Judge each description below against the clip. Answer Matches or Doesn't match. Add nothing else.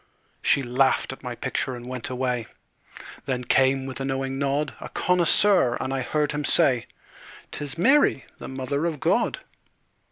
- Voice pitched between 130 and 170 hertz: Matches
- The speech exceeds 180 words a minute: Doesn't match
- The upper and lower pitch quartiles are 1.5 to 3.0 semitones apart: Matches